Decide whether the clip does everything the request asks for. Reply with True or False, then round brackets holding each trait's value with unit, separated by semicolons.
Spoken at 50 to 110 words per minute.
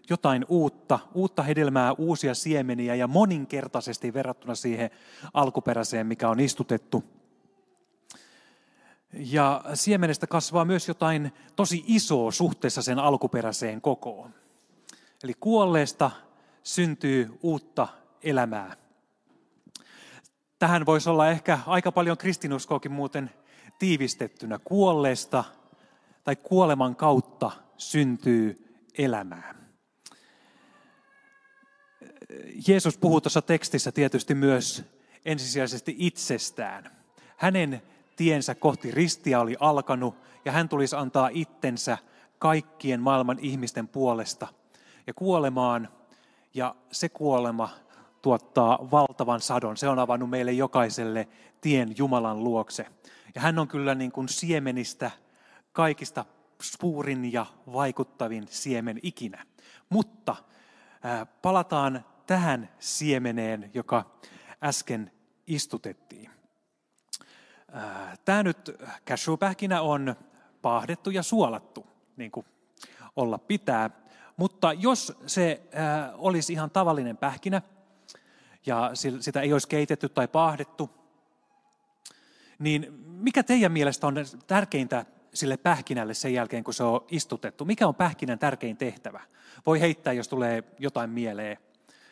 True (100 wpm)